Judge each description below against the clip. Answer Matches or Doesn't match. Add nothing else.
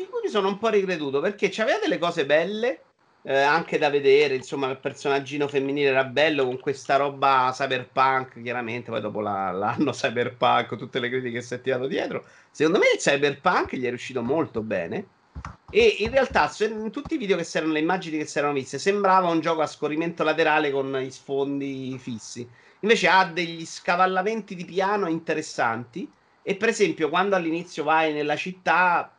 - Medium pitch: Matches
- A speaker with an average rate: Doesn't match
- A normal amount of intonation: Doesn't match